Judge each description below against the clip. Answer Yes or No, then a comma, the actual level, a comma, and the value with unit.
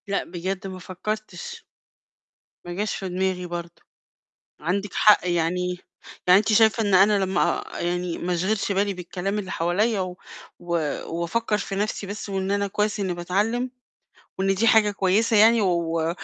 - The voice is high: Yes, high, 195 Hz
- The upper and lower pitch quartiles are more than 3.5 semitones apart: No, average, 2.8 semitones